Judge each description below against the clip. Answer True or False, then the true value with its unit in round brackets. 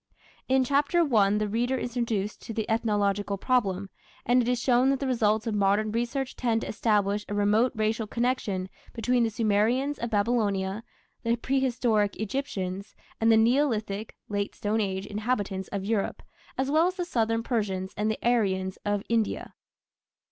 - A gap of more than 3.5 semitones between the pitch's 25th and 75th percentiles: False (3.2 semitones)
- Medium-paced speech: True (170 wpm)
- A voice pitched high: True (220 Hz)